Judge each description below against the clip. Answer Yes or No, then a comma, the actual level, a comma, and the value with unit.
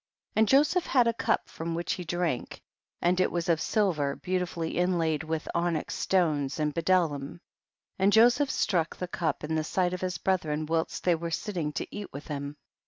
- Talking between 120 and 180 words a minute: No, average, 190 wpm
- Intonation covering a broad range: No, average, 2.8 semitones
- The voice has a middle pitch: Yes, medium, 170 Hz